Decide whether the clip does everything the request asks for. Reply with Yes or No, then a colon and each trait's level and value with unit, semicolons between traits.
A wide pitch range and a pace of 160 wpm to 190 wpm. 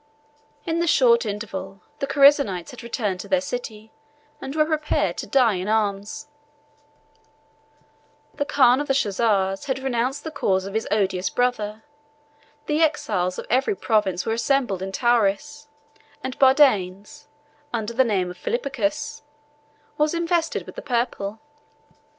No: wide, 5.8 semitones; average, 140 wpm